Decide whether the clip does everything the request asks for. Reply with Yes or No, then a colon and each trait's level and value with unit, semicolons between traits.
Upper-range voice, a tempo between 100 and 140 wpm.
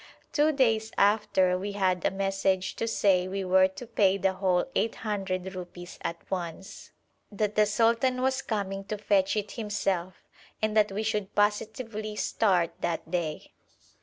No: high, 200 Hz; average, 155 wpm